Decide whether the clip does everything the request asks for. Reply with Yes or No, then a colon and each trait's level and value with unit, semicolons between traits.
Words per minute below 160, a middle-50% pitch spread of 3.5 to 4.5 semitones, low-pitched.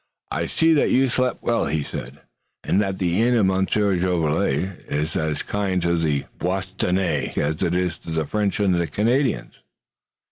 No: average, 175 wpm; average, 4.1 semitones; very low, 95 Hz